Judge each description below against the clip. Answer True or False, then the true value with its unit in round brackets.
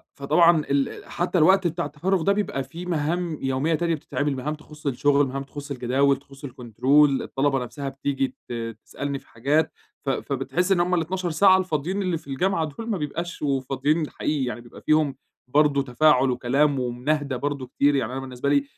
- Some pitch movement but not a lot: True (3.4 semitones)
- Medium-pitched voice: True (145 Hz)